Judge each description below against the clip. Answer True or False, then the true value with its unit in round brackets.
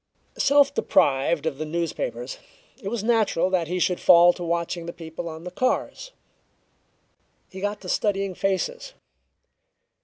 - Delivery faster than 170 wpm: False (145 wpm)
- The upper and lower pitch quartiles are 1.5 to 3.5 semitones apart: False (4.1 semitones)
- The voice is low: False (180 Hz)